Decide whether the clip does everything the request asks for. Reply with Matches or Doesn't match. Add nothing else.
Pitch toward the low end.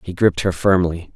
Matches